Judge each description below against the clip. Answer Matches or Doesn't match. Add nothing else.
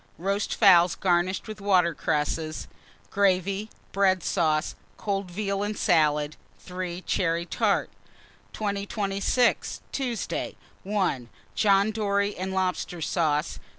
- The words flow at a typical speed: Doesn't match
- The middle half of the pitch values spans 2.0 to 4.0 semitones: Matches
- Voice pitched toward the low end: Doesn't match